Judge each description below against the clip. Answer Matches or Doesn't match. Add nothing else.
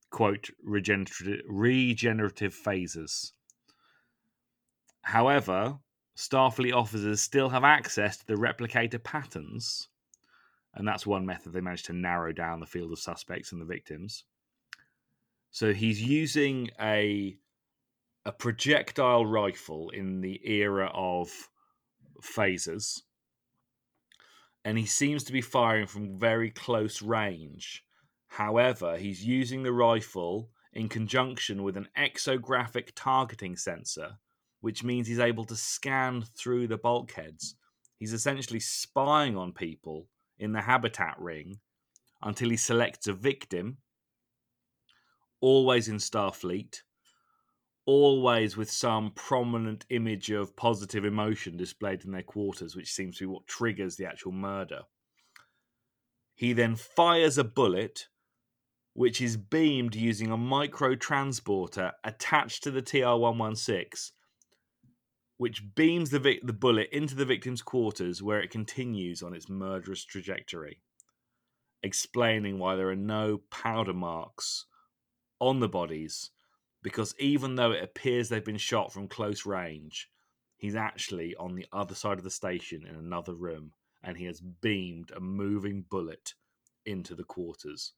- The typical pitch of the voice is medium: Doesn't match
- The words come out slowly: Matches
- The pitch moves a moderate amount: Matches